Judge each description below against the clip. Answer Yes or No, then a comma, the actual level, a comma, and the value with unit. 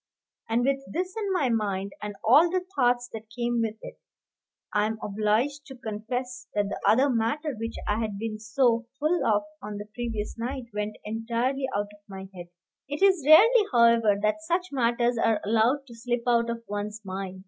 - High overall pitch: Yes, high, 230 Hz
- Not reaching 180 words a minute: No, average, 190 wpm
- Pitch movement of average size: Yes, average, 4.0 semitones